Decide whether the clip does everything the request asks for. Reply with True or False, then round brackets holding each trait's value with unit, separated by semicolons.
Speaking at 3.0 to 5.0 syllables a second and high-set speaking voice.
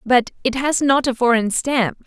True (4.4 syllables/s; 250 Hz)